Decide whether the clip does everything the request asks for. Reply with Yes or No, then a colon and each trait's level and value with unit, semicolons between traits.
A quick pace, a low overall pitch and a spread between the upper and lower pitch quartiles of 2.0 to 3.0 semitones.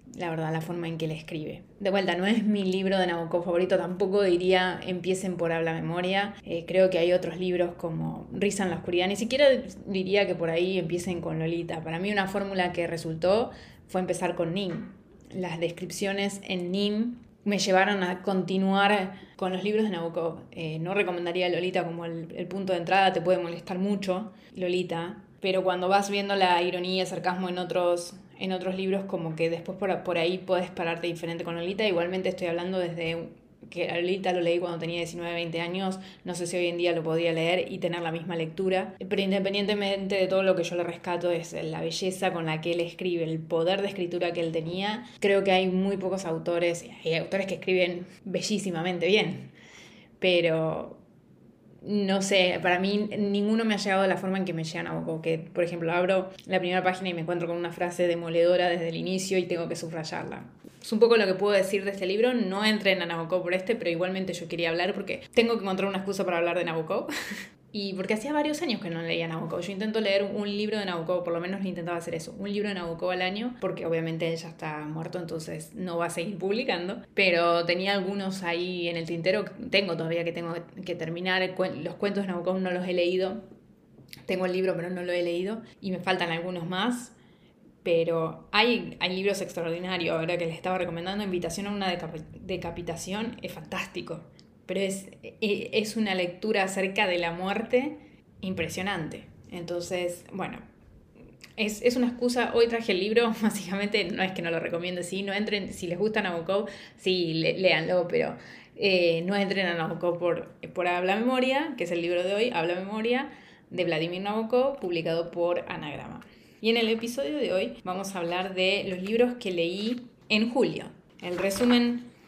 No: fast, 200 wpm; medium, 185 Hz; narrow, 2.4 semitones